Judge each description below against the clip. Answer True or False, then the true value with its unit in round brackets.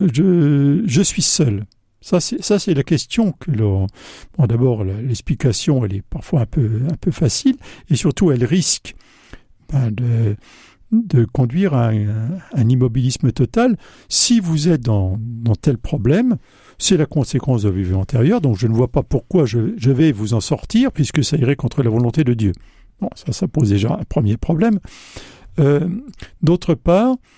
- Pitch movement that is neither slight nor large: False (6.7 semitones)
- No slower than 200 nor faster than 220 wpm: False (175 wpm)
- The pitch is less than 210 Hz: True (140 Hz)